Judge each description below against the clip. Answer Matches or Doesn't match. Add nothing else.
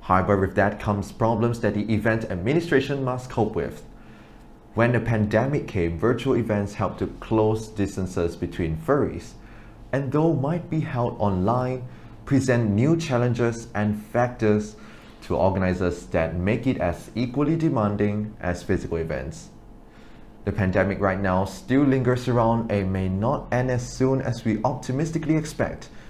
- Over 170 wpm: Doesn't match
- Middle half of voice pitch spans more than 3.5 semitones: Matches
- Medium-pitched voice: Doesn't match